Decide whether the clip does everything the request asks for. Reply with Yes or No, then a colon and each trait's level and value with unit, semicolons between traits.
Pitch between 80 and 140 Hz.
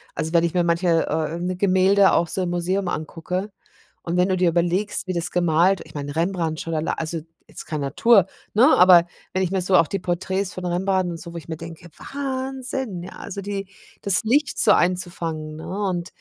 No: medium, 180 Hz